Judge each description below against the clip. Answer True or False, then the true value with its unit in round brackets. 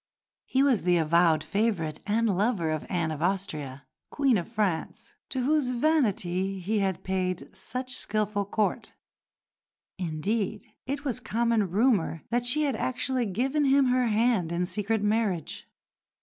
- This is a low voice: False (210 Hz)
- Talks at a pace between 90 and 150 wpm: True (145 wpm)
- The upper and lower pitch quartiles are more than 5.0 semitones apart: True (5.6 semitones)